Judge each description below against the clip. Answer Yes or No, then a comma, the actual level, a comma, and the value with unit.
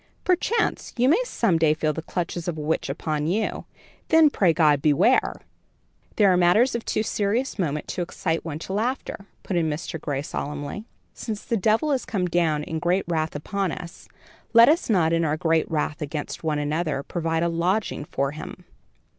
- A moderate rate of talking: Yes, average, 190 wpm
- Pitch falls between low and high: Yes, medium, 170 Hz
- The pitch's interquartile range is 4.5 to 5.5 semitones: Yes, average, 5.1 semitones